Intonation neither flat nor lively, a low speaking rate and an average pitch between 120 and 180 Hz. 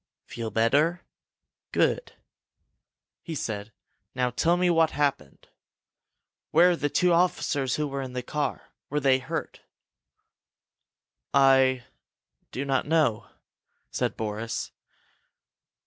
Yes: average, 4.7 semitones; slow, 110 wpm; low, 135 Hz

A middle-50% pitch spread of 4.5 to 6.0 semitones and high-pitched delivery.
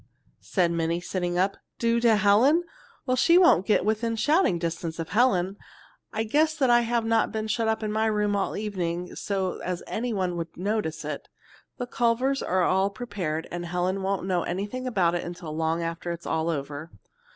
Yes: average, 4.8 semitones; high, 195 Hz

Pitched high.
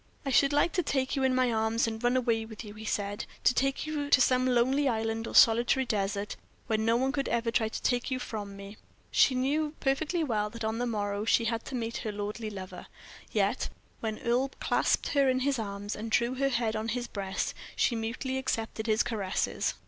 Yes: high, 230 Hz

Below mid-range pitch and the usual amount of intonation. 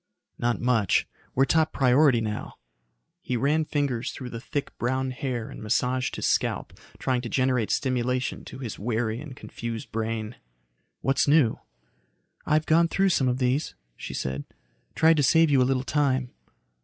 Yes: low, 130 Hz; average, 3.2 semitones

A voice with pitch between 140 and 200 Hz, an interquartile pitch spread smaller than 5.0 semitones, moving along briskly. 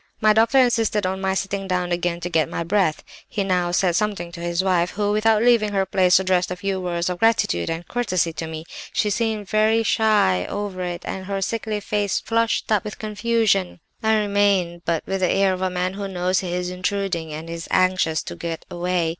Yes: high, 190 Hz; average, 3.0 semitones; fast, 215 wpm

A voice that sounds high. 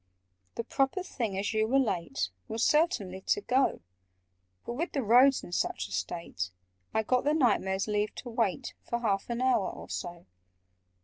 Yes: high, 225 Hz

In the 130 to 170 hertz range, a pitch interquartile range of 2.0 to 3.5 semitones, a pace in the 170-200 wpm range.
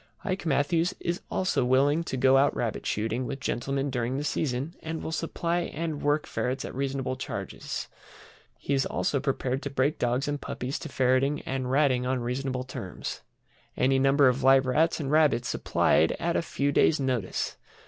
Yes: low, 135 Hz; narrow, 2.5 semitones; average, 180 wpm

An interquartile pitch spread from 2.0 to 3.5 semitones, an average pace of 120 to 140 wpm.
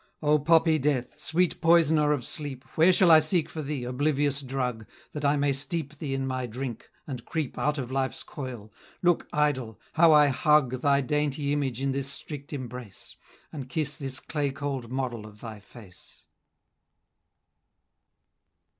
No: average, 2.8 semitones; average, 160 wpm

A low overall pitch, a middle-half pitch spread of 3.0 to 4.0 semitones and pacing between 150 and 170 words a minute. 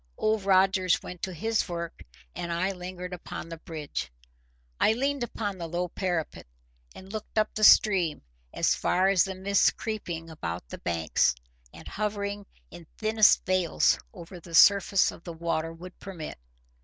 No: medium, 185 Hz; average, 3.3 semitones; average, 160 wpm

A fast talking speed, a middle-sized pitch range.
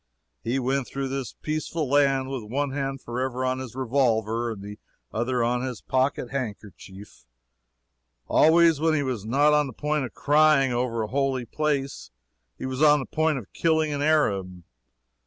No: average, 170 wpm; average, 3.4 semitones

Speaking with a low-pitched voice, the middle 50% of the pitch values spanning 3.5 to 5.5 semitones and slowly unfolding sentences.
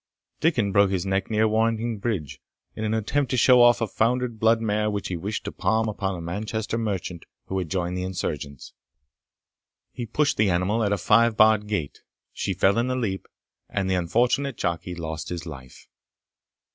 No: low, 105 Hz; average, 3.8 semitones; average, 185 wpm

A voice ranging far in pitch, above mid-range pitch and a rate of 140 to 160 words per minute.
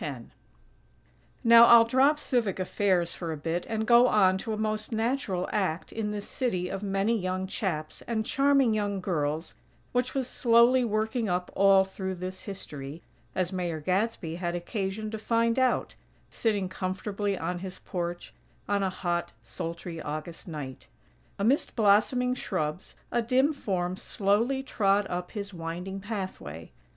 No: average, 4.1 semitones; high, 195 Hz; average, 150 wpm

